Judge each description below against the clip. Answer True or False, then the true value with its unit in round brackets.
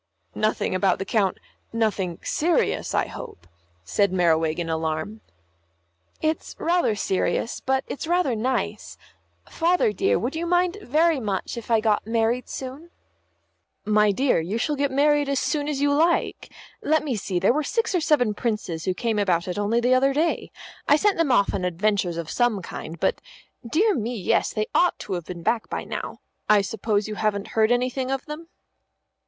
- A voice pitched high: True (230 Hz)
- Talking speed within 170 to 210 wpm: True (180 wpm)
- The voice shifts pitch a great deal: True (6.6 semitones)